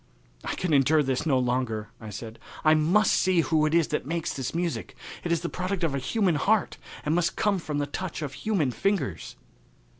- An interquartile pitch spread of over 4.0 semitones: Yes, average, 4.9 semitones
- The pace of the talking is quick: Yes, fast, 210 wpm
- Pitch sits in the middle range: Yes, medium, 155 Hz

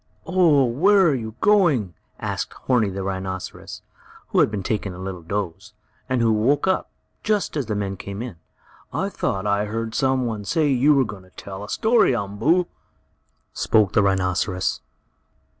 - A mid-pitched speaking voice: No, low, 110 Hz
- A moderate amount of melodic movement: No, wide, 6.0 semitones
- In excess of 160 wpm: Yes, average, 170 wpm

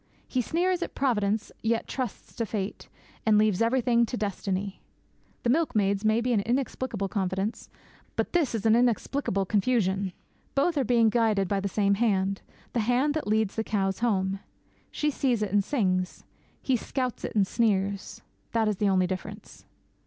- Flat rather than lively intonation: No, average, 3.7 semitones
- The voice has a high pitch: Yes, high, 215 Hz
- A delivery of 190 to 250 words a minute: No, average, 165 wpm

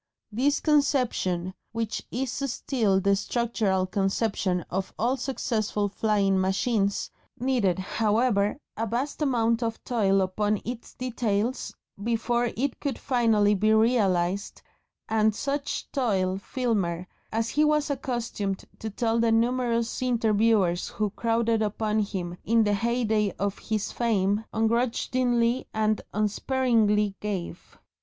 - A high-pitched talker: Yes, high, 220 Hz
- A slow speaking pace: Yes, slow, 120 wpm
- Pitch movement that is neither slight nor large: Yes, average, 3.2 semitones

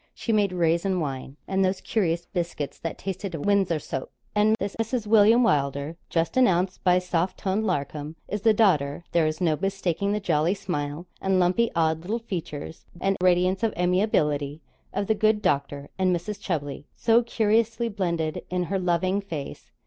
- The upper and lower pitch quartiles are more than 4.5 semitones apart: No, average, 4.2 semitones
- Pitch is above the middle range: No, medium, 180 Hz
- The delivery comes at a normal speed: Yes, average, 170 wpm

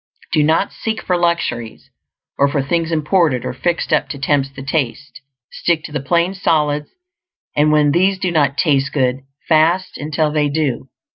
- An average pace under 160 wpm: No, average, 170 wpm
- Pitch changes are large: No, average, 3.3 semitones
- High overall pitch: No, medium, 150 Hz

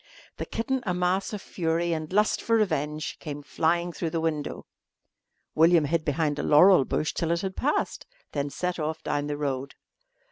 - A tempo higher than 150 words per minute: Yes, average, 180 wpm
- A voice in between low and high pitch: Yes, medium, 165 Hz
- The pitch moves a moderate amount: Yes, average, 3.3 semitones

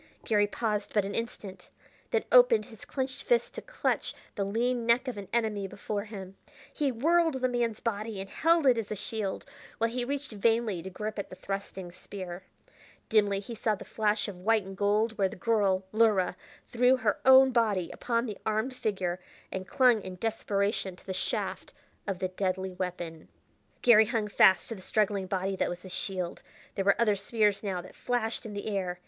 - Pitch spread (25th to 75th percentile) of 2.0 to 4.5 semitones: Yes, average, 3.3 semitones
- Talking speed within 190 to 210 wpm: Yes, average, 195 wpm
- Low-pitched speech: No, high, 210 Hz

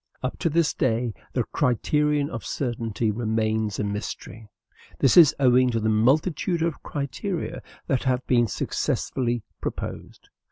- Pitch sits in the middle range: No, low, 125 Hz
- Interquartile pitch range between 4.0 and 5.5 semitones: Yes, average, 4.5 semitones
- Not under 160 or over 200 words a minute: No, slow, 135 wpm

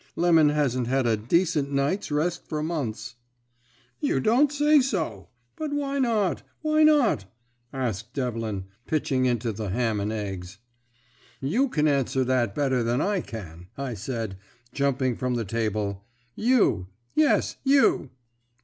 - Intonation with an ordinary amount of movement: No, wide, 7.7 semitones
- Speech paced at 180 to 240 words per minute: No, average, 140 wpm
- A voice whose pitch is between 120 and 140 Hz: Yes, low, 135 Hz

